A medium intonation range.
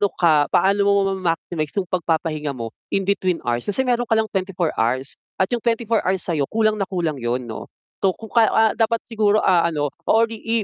No: wide, 6.0 semitones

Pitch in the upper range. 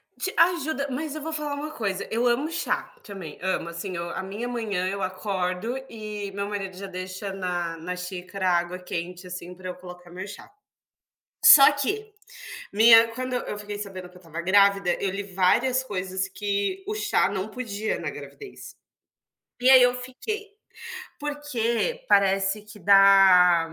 Yes: high, 200 Hz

